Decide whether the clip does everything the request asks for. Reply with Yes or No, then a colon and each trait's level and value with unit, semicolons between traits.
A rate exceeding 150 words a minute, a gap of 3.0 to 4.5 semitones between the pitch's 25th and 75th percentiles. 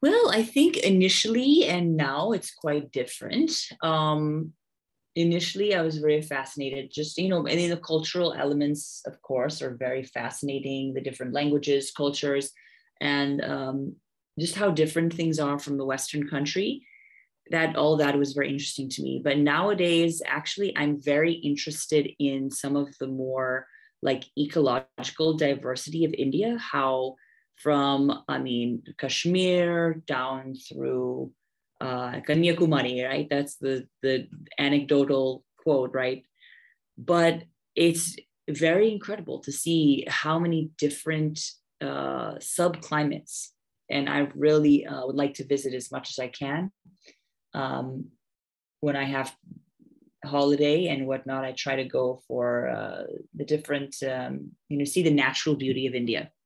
No: average, 140 wpm; average, 3.7 semitones